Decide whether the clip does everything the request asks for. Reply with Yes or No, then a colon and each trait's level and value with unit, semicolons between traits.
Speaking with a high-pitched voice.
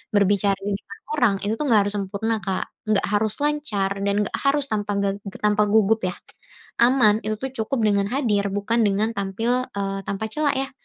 Yes: high, 210 Hz